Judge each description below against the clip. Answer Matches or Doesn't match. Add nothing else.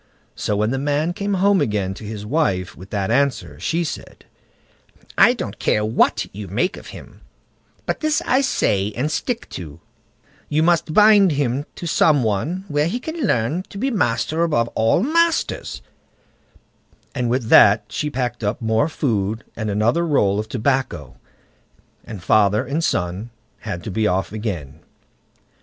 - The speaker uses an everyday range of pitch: Doesn't match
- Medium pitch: Doesn't match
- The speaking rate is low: Doesn't match